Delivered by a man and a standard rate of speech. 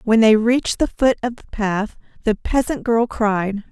No: female; average, 195 wpm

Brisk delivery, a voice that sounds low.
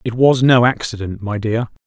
No: average, 195 wpm; low, 115 Hz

